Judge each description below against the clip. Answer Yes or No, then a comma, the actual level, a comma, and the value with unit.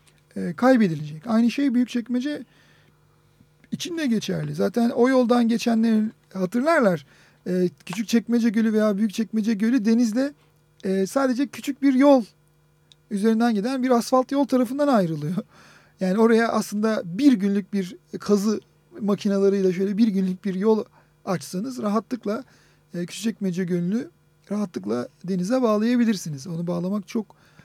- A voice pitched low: No, high, 215 Hz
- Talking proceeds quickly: No, average, 130 wpm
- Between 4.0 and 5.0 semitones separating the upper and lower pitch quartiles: Yes, average, 4.5 semitones